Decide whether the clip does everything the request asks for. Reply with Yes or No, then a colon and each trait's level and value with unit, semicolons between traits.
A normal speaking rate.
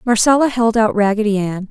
Yes: average, 175 wpm